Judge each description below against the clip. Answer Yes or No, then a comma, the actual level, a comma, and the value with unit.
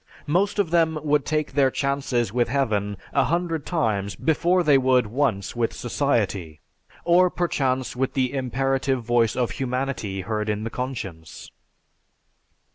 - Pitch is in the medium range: No, low, 130 Hz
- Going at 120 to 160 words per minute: Yes, average, 140 wpm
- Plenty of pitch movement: No, average, 4.6 semitones